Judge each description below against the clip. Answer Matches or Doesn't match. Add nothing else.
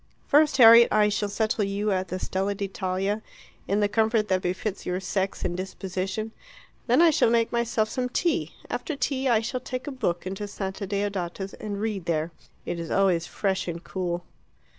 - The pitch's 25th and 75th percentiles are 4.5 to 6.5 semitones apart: Doesn't match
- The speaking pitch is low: Doesn't match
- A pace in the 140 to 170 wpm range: Doesn't match